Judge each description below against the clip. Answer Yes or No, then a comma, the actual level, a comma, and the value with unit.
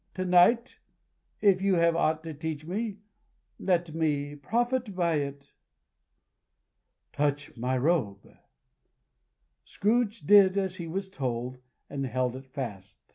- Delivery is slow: Yes, slow, 125 wpm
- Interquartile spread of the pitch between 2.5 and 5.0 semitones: No, wide, 5.6 semitones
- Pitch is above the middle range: No, medium, 160 Hz